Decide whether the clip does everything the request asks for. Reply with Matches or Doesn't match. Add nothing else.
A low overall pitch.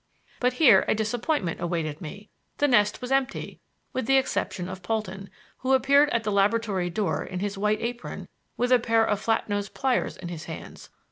Doesn't match